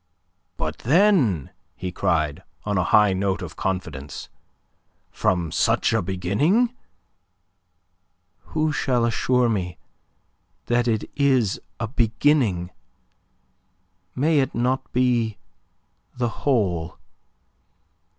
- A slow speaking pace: Yes, slow, 95 wpm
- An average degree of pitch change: No, wide, 6.2 semitones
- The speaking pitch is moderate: No, low, 110 Hz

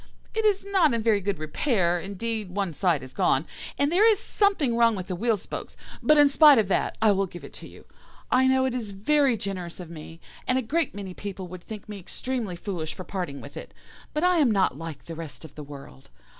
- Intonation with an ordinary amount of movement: No, wide, 7.0 semitones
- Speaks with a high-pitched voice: Yes, high, 200 Hz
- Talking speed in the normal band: No, fast, 235 wpm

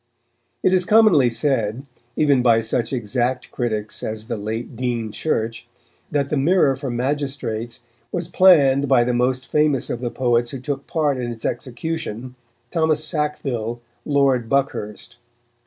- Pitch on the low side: Yes, low, 130 Hz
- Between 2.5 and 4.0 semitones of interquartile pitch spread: Yes, average, 3.6 semitones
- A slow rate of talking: No, average, 145 wpm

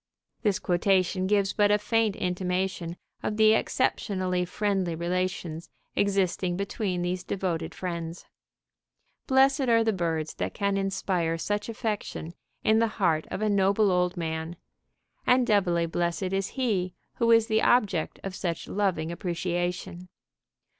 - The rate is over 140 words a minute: No, slow, 135 wpm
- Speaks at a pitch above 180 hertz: Yes, high, 190 Hz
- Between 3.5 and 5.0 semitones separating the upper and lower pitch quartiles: No, average, 3.0 semitones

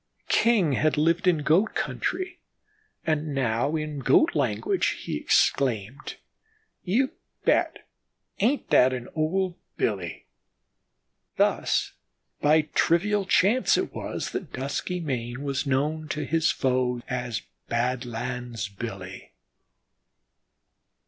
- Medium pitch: Yes, medium, 145 Hz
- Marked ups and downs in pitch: Yes, wide, 5.8 semitones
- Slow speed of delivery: Yes, slow, 105 wpm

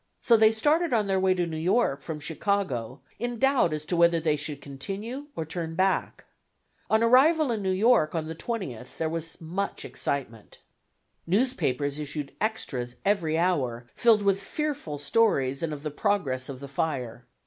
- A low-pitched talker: No, medium, 170 Hz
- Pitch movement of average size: No, wide, 7.1 semitones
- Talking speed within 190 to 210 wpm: No, average, 170 wpm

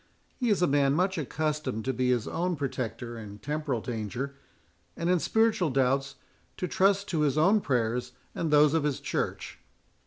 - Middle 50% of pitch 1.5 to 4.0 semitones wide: No, average, 5.2 semitones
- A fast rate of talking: No, average, 175 wpm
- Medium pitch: Yes, medium, 145 Hz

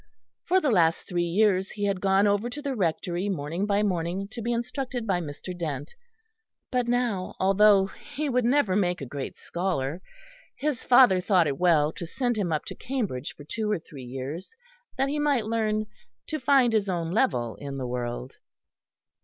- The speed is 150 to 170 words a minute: No, average, 185 wpm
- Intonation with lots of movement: Yes, wide, 6.2 semitones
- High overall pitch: Yes, high, 195 Hz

